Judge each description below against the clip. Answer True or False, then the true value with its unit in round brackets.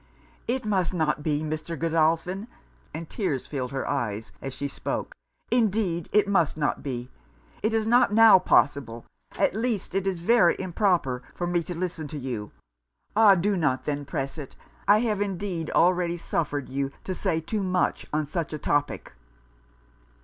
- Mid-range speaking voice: True (170 Hz)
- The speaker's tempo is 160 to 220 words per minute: True (165 wpm)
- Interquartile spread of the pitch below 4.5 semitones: False (5.2 semitones)